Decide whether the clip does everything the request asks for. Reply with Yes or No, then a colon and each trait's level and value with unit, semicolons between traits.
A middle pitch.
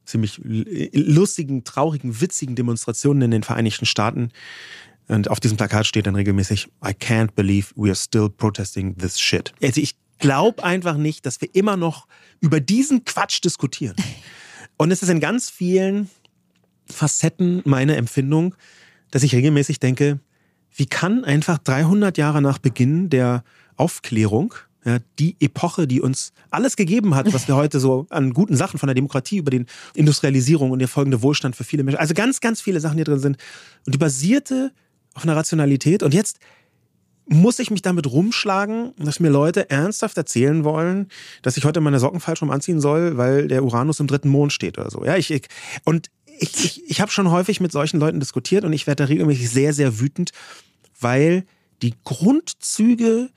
Yes: medium, 145 Hz